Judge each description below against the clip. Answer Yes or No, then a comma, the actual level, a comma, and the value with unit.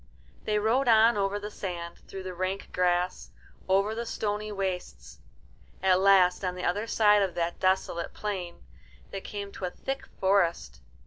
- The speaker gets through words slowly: No, average, 165 wpm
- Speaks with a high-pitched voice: Yes, high, 195 Hz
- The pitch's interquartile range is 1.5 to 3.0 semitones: Yes, narrow, 2.5 semitones